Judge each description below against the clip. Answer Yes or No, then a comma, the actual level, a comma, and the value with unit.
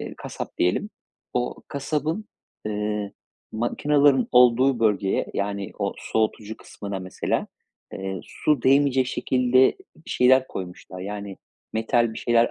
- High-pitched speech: No, low, 115 Hz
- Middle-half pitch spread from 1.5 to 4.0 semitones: No, average, 4.4 semitones